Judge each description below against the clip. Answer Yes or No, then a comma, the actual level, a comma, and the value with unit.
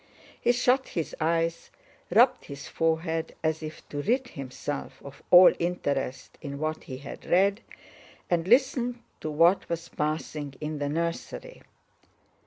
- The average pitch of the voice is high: No, medium, 165 Hz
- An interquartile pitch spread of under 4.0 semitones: No, average, 4.9 semitones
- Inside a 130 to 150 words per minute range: Yes, average, 140 wpm